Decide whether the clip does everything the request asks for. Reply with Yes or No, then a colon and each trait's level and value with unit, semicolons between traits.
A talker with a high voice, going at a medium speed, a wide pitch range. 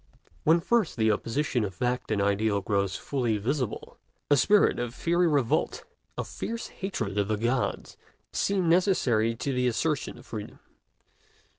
No: low, 125 Hz; average, 150 wpm; wide, 6.8 semitones